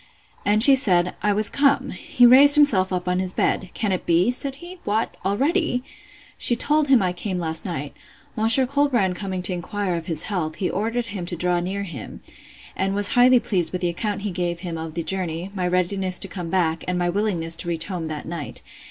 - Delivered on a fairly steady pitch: No, average, 4.3 semitones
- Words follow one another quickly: Yes, fast, 210 wpm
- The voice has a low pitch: No, high, 190 Hz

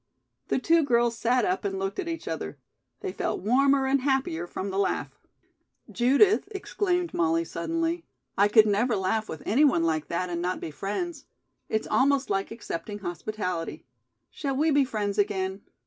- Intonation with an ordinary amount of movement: No, wide, 6.6 semitones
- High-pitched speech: Yes, high, 215 Hz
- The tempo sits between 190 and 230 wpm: No, average, 170 wpm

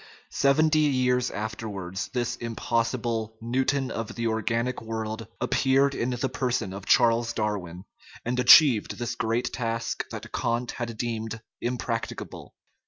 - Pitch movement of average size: No, narrow, 2.1 semitones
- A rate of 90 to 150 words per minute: Yes, slow, 135 wpm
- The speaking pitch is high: No, low, 115 Hz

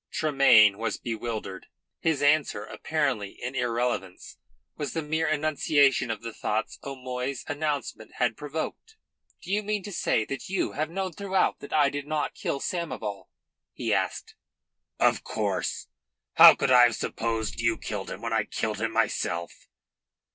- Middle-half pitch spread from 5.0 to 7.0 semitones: Yes, average, 5.3 semitones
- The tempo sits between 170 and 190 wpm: No, average, 155 wpm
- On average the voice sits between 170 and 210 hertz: No, medium, 140 Hz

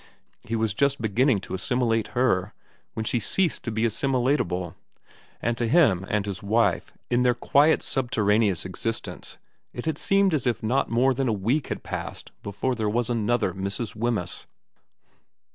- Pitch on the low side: Yes, low, 115 Hz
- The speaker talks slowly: No, average, 160 wpm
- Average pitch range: Yes, average, 3.6 semitones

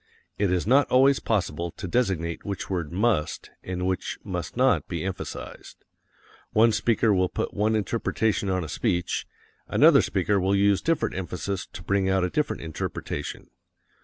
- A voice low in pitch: Yes, very low, 95 Hz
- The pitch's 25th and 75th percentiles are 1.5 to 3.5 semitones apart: Yes, average, 3.2 semitones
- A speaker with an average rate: Yes, average, 160 wpm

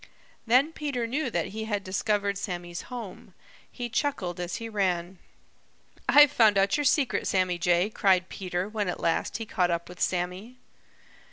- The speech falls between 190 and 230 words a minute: No, average, 165 wpm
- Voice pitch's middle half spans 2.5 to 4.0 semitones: No, average, 4.5 semitones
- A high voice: Yes, high, 200 Hz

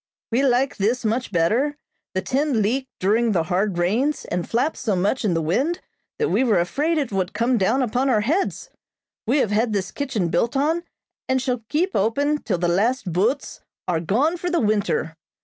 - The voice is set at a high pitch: Yes, high, 230 Hz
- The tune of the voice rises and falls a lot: Yes, wide, 6.1 semitones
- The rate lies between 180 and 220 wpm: Yes, average, 195 wpm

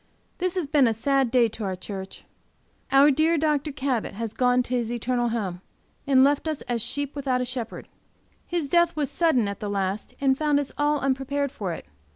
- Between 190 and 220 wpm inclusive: Yes, average, 200 wpm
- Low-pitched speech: No, very high, 265 Hz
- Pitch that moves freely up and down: No, average, 3.9 semitones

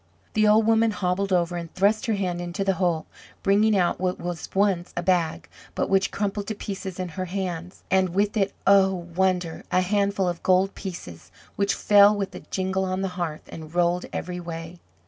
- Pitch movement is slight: Yes, narrow, 2.2 semitones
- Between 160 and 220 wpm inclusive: Yes, average, 195 wpm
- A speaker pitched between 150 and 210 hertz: Yes, medium, 185 Hz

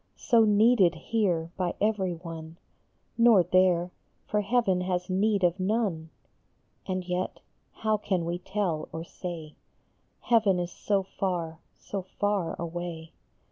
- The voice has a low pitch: No, medium, 185 Hz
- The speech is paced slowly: Yes, slow, 130 wpm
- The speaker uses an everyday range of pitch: Yes, average, 3.2 semitones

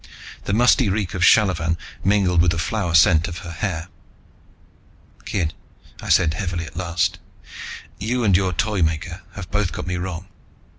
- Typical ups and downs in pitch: Yes, average, 3.0 semitones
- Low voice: Yes, very low, 90 Hz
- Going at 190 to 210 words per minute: No, average, 155 wpm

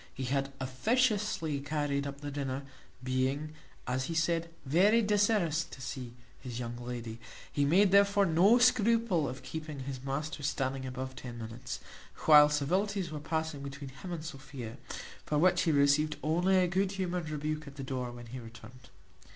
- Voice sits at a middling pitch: Yes, medium, 145 Hz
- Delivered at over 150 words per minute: Yes, average, 165 wpm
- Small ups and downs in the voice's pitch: No, average, 4.9 semitones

